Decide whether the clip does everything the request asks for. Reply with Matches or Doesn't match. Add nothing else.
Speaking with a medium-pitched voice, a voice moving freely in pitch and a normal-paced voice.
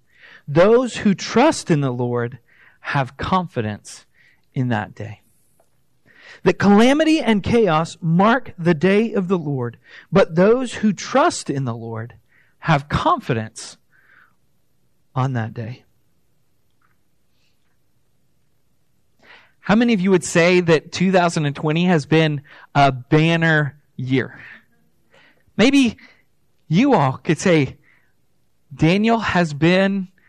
Doesn't match